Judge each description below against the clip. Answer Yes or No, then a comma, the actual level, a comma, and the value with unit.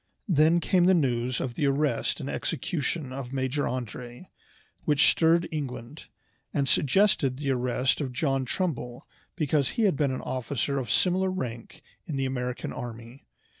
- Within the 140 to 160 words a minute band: Yes, average, 155 wpm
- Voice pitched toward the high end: No, low, 135 Hz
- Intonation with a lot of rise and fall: No, average, 4.0 semitones